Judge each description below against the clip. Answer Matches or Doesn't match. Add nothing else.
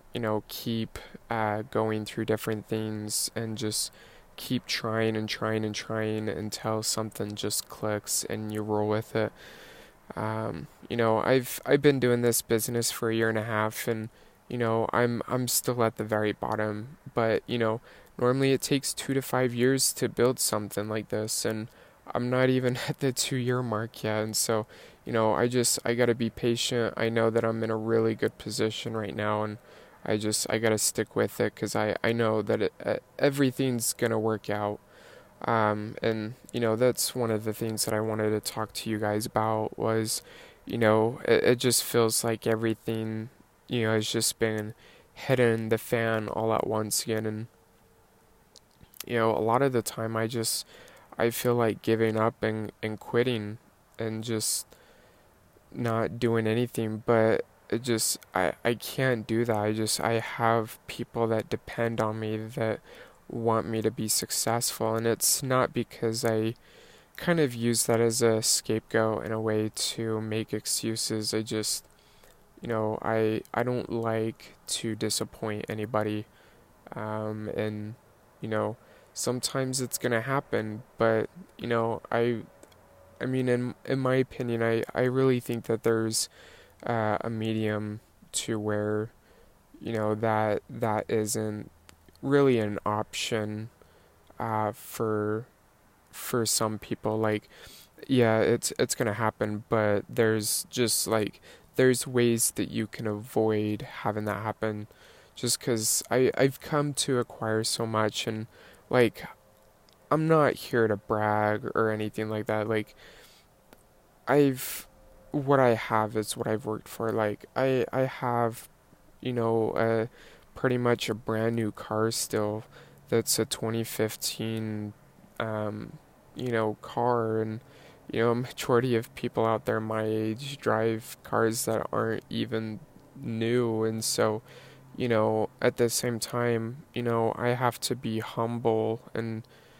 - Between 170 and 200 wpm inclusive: Doesn't match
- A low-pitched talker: Matches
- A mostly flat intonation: Matches